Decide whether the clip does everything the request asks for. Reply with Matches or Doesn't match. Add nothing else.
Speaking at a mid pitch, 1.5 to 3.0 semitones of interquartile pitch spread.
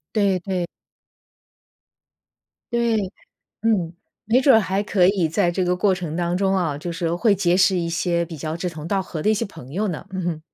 Matches